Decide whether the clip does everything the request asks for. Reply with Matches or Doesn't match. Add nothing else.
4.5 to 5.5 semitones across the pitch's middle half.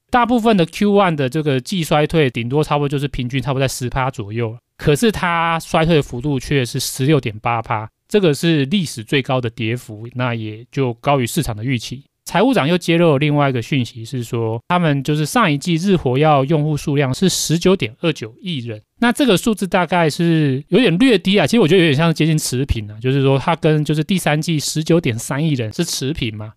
Matches